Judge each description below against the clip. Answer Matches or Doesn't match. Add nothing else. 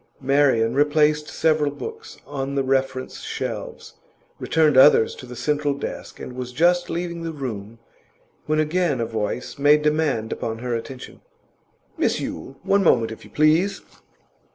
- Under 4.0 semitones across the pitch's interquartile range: Matches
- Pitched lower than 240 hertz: Matches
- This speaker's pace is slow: Doesn't match